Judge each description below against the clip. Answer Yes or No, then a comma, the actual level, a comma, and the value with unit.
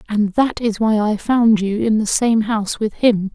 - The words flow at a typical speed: No, fast, 235 wpm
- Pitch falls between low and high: No, high, 215 Hz